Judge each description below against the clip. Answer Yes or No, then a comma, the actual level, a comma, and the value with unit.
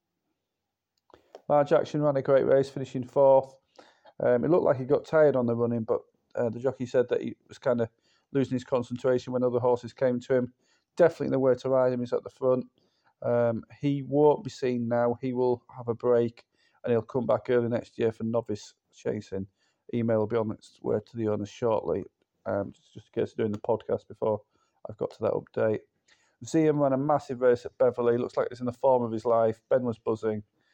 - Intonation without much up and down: Yes, narrow, 2.3 semitones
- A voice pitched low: Yes, low, 125 Hz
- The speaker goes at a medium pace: No, fast, 220 wpm